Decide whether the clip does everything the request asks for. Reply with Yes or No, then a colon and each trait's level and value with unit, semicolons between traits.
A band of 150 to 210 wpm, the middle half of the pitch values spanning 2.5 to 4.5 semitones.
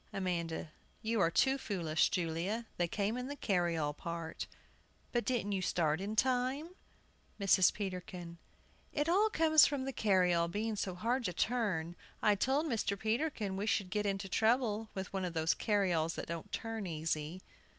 No: average, 165 wpm; average, 5.1 semitones